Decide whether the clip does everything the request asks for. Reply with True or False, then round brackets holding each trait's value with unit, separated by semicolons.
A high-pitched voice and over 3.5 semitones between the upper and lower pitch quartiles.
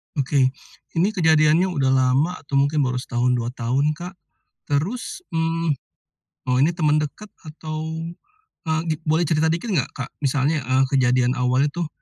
False (150 Hz; 3.9 semitones)